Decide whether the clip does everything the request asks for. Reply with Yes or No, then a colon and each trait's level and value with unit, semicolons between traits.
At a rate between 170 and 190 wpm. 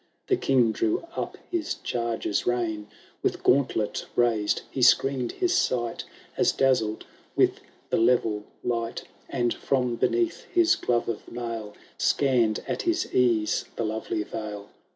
No: slow, 135 wpm